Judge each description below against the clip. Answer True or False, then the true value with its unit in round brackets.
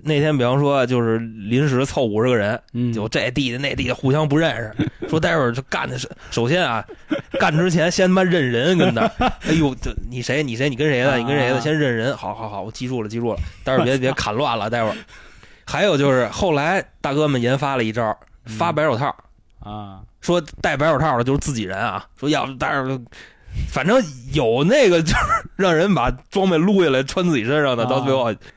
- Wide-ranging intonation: False (4.3 semitones)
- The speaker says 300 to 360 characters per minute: True (305 characters per minute)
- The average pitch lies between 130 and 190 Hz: True (135 Hz)